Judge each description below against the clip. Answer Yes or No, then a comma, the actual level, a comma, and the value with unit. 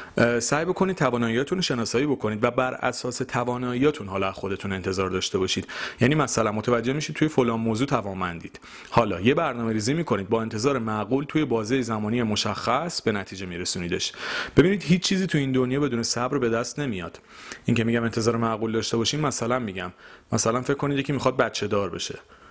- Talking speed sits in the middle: No, fast, 175 wpm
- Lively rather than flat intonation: No, average, 3.7 semitones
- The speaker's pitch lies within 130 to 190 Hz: No, low, 120 Hz